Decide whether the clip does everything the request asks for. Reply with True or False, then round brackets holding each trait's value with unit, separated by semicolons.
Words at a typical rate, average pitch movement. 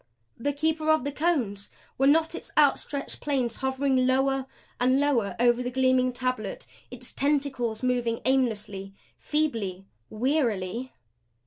False (125 wpm; 3.3 semitones)